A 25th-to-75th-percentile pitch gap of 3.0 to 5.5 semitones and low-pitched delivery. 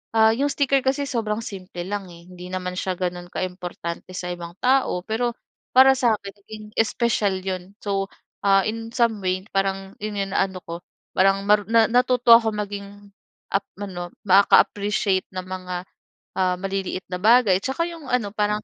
No: average, 3.4 semitones; high, 200 Hz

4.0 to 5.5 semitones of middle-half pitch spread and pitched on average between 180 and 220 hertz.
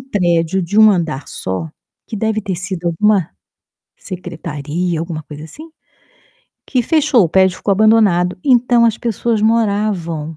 Yes: average, 4.7 semitones; high, 190 Hz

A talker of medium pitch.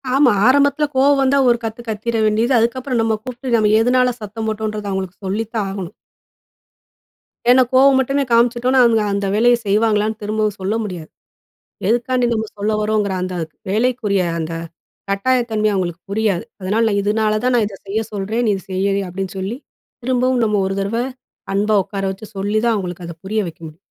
No: high, 215 Hz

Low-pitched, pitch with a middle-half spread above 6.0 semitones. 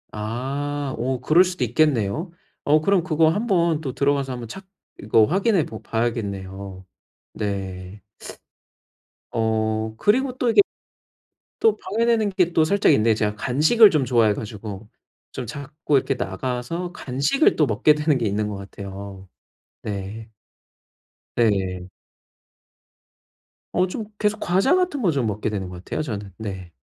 Yes: low, 125 Hz; wide, 8.1 semitones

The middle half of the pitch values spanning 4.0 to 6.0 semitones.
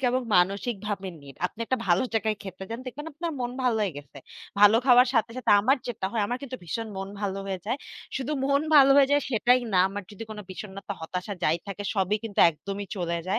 Yes: average, 4.3 semitones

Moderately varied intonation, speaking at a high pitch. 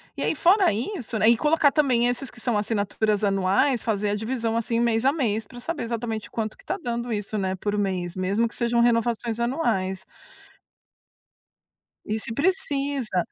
Yes: average, 3.1 semitones; high, 230 Hz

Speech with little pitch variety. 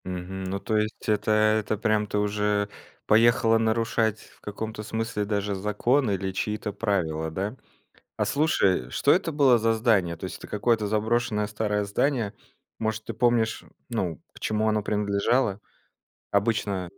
Yes: narrow, 1.9 semitones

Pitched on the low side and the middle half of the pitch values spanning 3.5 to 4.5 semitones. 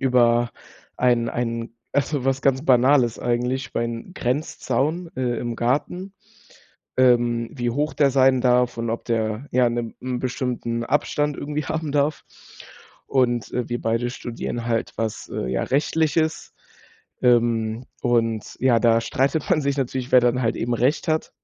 No: low, 125 Hz; average, 2.7 semitones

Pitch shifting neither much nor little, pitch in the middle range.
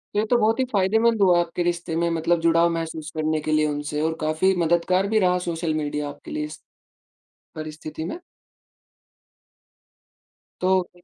Yes: average, 3.0 semitones; medium, 170 Hz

